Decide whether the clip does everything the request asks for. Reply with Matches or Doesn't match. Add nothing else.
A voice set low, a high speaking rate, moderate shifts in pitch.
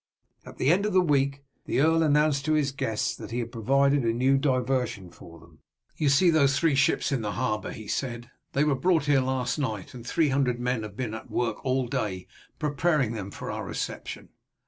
Matches